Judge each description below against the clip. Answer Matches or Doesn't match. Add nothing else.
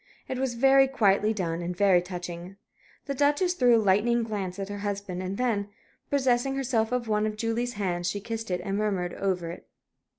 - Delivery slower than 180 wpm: Doesn't match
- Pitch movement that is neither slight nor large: Matches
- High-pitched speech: Matches